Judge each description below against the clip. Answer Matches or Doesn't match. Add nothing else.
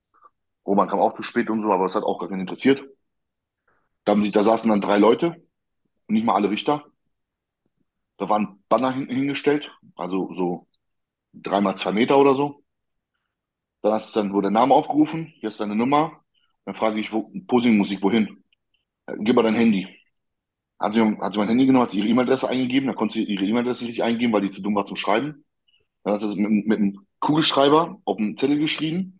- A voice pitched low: Matches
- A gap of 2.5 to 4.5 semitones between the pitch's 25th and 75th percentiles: Doesn't match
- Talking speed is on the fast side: Matches